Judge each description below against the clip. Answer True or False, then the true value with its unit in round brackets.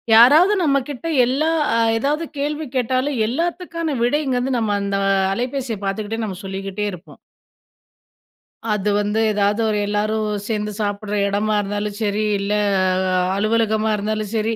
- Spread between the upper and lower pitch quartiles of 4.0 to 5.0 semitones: True (4.3 semitones)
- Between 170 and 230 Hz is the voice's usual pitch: True (220 Hz)